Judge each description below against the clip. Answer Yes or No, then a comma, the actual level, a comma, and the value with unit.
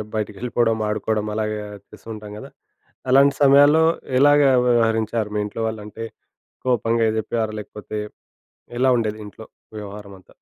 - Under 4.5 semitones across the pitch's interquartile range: Yes, narrow, 2.4 semitones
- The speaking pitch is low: Yes, low, 110 Hz